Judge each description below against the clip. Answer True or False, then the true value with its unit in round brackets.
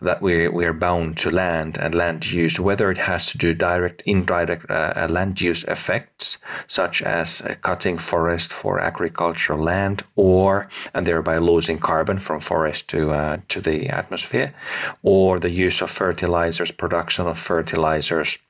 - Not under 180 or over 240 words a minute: False (160 wpm)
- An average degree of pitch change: False (1.7 semitones)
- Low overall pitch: True (85 Hz)